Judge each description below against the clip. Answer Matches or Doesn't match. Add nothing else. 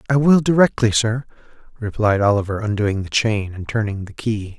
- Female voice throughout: Doesn't match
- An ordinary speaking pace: Matches